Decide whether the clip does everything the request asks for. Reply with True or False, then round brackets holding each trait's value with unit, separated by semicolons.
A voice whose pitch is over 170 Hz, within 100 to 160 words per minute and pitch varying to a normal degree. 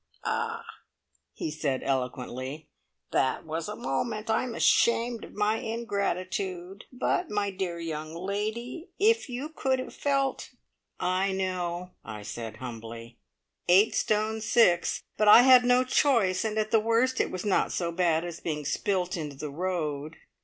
False (190 Hz; 155 wpm; 6.3 semitones)